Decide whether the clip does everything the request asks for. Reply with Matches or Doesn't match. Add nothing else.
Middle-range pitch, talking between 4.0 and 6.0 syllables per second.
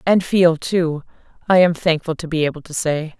Matches